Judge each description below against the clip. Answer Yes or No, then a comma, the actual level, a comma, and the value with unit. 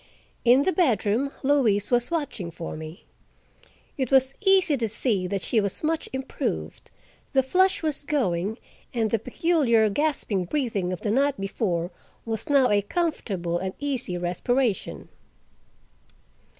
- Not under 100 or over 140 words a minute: Yes, slow, 135 wpm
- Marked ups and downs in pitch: Yes, wide, 6.5 semitones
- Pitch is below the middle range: No, high, 235 Hz